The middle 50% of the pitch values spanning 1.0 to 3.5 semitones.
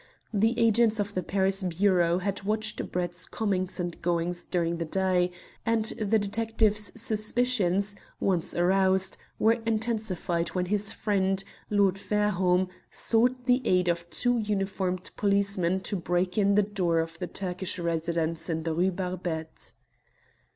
Yes: average, 2.9 semitones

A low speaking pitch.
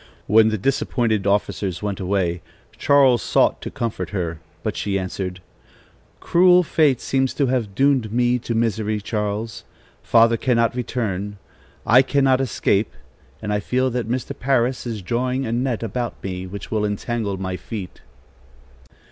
Yes: low, 115 Hz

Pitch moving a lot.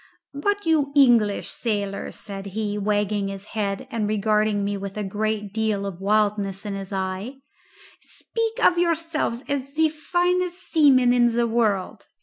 Yes: wide, 5.8 semitones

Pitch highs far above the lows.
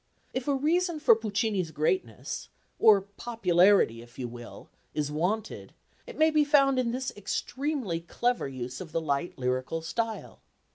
Yes: wide, 8.9 semitones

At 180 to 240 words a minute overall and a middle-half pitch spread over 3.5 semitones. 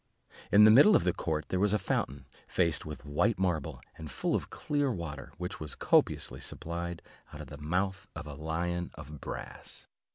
Yes: average, 190 wpm; average, 3.9 semitones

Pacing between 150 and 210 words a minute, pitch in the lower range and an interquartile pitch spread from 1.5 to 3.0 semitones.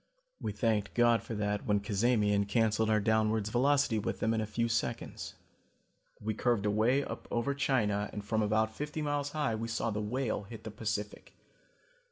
Yes: average, 180 wpm; low, 110 Hz; narrow, 2.4 semitones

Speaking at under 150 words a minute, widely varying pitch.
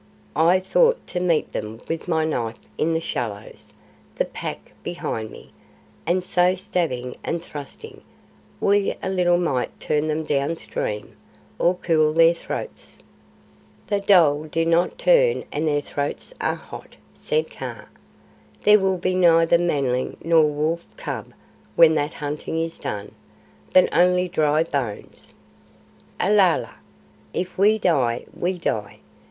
No: slow, 135 wpm; average, 3.8 semitones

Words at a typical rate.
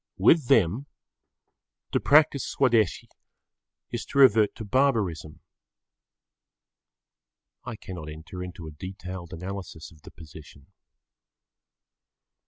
No: slow, 95 wpm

